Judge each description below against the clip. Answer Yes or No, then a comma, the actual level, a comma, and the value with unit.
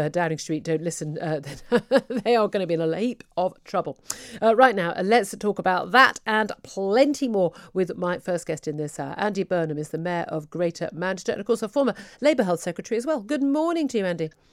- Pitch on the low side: No, medium, 185 Hz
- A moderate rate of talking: No, fast, 225 wpm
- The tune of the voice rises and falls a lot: Yes, wide, 5.7 semitones